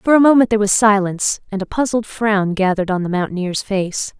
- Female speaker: Yes, female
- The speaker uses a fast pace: Yes, fast, 215 wpm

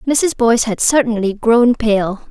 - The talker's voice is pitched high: Yes, high, 230 Hz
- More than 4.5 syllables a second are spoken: No, 4.0 syllables/s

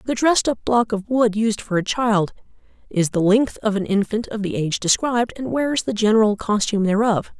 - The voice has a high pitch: Yes, high, 215 Hz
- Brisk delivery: Yes, fast, 210 wpm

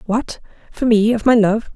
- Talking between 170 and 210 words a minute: Yes, fast, 205 wpm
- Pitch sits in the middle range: No, high, 225 Hz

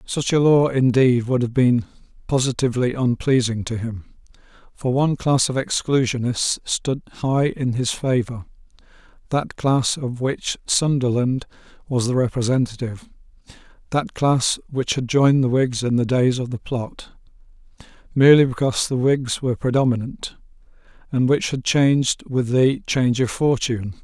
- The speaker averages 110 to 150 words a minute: Yes, average, 140 wpm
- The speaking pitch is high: No, low, 130 Hz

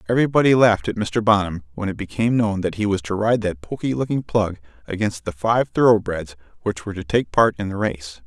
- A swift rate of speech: Yes, fast, 220 wpm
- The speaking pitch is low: Yes, low, 100 Hz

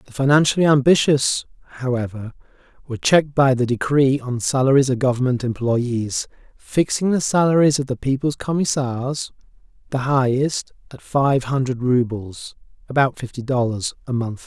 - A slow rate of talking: Yes, slow, 125 wpm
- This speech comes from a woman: No, male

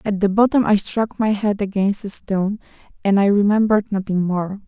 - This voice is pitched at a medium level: No, high, 205 Hz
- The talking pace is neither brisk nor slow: Yes, average, 190 wpm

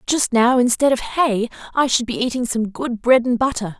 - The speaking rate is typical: No, fast, 220 wpm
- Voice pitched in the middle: No, high, 240 Hz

